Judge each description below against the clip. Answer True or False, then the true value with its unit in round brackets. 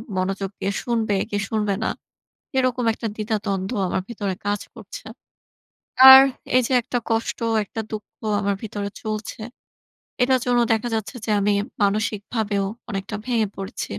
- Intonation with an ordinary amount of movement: False (2.2 semitones)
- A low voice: False (215 Hz)